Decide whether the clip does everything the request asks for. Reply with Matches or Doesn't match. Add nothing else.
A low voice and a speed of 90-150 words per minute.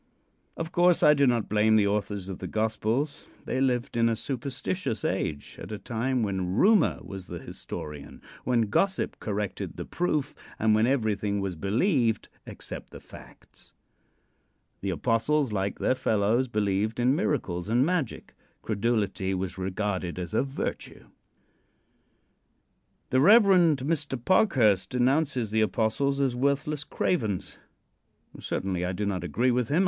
Matches